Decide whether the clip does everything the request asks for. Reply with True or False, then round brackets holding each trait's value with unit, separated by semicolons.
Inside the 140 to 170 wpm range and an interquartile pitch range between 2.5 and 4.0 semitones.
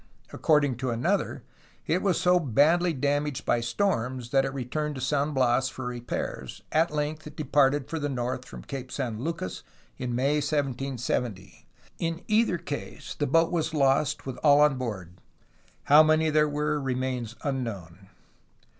True (155 wpm; 3.4 semitones)